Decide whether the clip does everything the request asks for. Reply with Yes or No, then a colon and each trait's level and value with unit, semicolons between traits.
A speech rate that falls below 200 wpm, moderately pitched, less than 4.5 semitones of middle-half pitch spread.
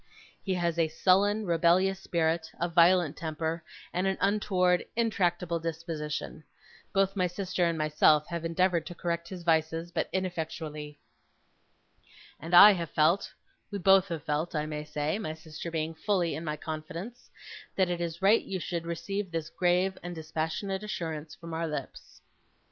Yes: average, 160 wpm; medium, 170 Hz; average, 2.7 semitones